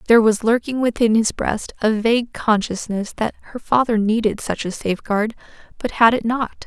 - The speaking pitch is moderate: No, high, 225 Hz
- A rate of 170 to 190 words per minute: Yes, average, 180 wpm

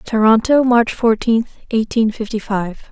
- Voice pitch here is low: No, high, 225 Hz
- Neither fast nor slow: No, slow, 125 wpm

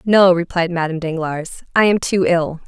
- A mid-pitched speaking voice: Yes, medium, 175 Hz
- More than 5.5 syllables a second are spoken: No, 5.2 syllables/s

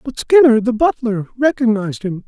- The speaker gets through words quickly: No, slow, 105 wpm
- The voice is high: Yes, high, 235 Hz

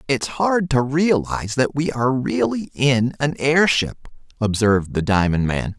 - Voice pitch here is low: Yes, low, 130 Hz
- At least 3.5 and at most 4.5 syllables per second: Yes, 4.4 syllables/s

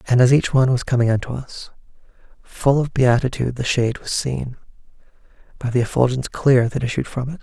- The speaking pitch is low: Yes, low, 125 Hz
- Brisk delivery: No, average, 185 wpm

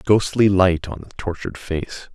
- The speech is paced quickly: No, average, 170 wpm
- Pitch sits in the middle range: No, very low, 90 Hz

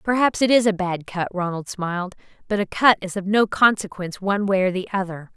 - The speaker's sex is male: No, female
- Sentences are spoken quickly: Yes, fast, 225 wpm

